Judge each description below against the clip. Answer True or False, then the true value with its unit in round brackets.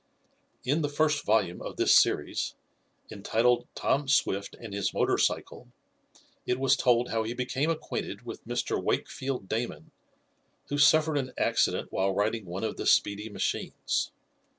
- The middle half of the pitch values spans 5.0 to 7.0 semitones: True (5.3 semitones)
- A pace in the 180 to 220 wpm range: False (150 wpm)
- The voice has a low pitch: True (120 Hz)